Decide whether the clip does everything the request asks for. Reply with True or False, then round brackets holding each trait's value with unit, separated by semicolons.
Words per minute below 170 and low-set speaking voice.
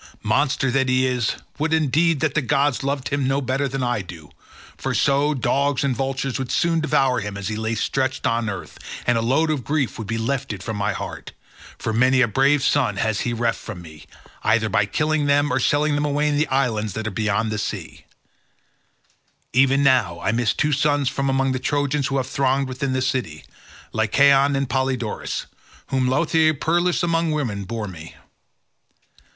False (190 wpm; 130 Hz)